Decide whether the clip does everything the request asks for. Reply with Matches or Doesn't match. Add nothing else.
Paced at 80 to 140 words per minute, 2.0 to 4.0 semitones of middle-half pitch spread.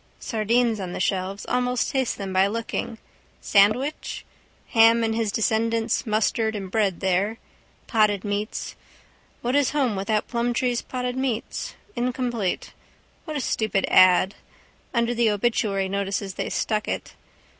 Matches